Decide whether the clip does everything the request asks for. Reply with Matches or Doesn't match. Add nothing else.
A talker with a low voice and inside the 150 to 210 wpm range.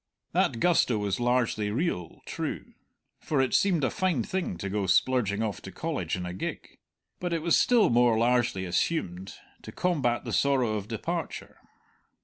Matches